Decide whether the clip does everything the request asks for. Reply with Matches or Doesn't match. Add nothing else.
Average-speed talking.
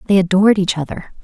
Matches